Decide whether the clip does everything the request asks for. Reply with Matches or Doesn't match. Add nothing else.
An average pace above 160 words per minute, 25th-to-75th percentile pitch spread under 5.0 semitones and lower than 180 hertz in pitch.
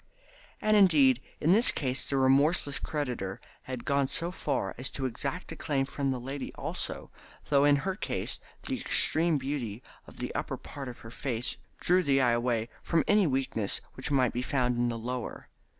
Matches